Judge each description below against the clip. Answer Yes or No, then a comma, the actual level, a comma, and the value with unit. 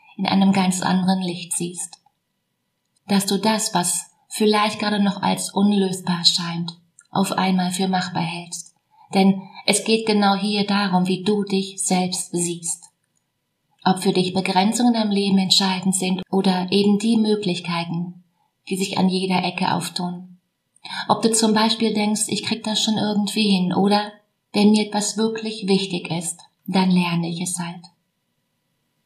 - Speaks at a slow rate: No, average, 150 wpm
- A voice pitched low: No, high, 190 Hz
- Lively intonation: No, narrow, 2.5 semitones